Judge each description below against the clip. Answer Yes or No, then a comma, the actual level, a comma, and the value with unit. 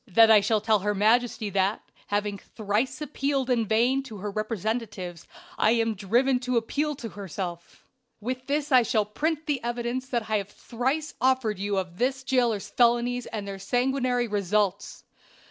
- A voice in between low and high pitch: No, high, 230 Hz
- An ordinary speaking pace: Yes, average, 165 wpm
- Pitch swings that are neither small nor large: Yes, average, 3.7 semitones